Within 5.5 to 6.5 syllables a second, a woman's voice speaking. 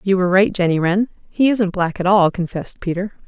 Yes: 5.8 syllables/s; female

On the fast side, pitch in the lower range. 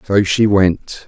No: average, 170 wpm; very low, 95 Hz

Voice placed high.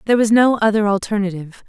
Yes: high, 210 Hz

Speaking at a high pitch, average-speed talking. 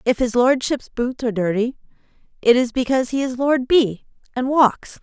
Yes: very high, 250 Hz; average, 180 wpm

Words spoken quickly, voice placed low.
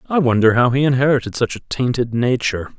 No: average, 195 wpm; low, 125 Hz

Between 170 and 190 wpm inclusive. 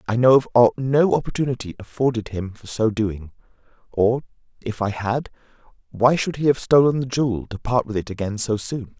Yes: average, 185 wpm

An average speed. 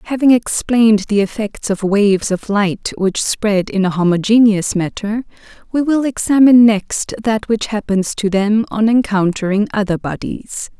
Yes: average, 150 wpm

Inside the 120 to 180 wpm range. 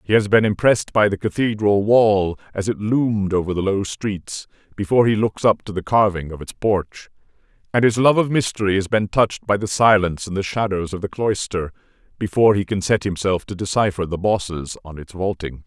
No: fast, 205 wpm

